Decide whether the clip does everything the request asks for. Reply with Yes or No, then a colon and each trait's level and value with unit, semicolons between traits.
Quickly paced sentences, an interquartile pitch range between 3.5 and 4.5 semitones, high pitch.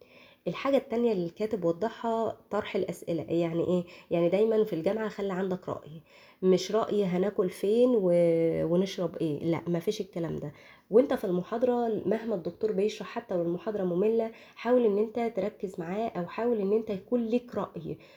Yes: fast, 160 wpm; average, 4.2 semitones; high, 205 Hz